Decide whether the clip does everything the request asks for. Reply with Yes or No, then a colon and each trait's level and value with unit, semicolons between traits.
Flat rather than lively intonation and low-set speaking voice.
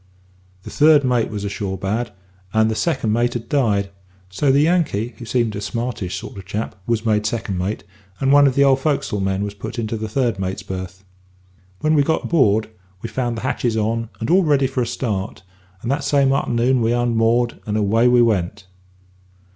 No: average, 4.0 semitones; low, 115 Hz